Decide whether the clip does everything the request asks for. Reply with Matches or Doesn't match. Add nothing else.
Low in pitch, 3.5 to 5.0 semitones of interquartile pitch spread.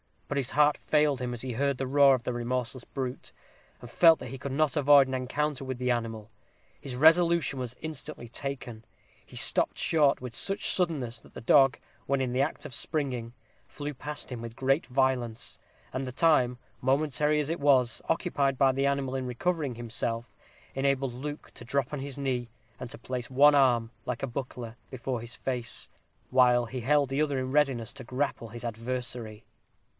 Doesn't match